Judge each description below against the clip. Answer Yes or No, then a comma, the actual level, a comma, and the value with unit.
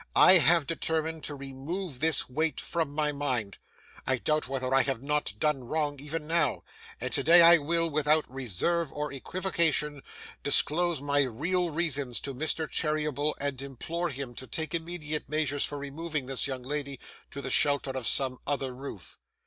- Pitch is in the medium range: Yes, medium, 145 Hz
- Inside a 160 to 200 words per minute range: Yes, average, 165 wpm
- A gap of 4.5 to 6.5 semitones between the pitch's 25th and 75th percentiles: No, average, 3.1 semitones